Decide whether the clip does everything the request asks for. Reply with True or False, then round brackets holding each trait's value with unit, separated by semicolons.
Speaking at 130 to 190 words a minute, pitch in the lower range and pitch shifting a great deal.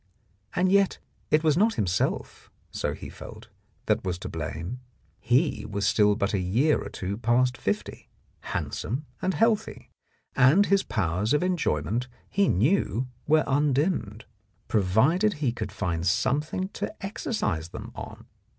True (150 wpm; 125 Hz; 8.4 semitones)